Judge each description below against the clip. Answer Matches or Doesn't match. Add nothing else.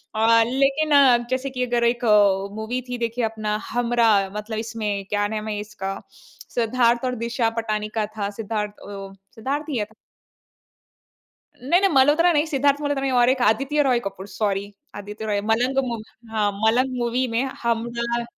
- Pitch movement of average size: Matches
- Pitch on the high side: Matches